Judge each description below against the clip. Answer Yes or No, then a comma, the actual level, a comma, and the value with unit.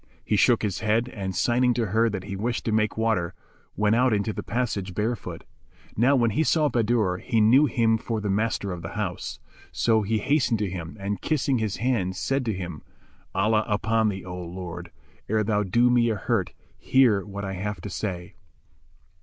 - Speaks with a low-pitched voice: Yes, low, 110 Hz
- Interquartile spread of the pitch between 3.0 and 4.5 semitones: Yes, average, 3.3 semitones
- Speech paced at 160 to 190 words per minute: No, average, 200 wpm